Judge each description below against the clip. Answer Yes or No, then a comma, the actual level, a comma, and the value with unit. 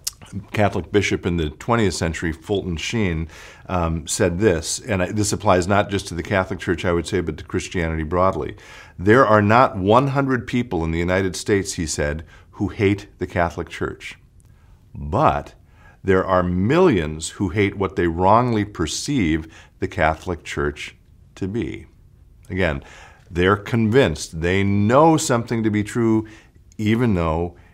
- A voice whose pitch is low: Yes, very low, 95 Hz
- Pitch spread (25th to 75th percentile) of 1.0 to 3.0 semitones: No, average, 3.5 semitones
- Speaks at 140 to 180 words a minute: Yes, average, 150 wpm